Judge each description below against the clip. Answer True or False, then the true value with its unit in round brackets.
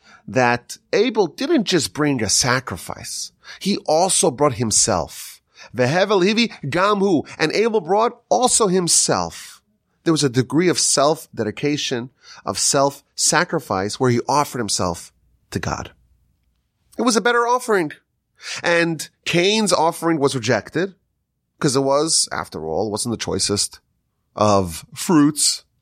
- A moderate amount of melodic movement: False (7.0 semitones)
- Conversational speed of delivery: False (130 wpm)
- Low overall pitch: False (145 Hz)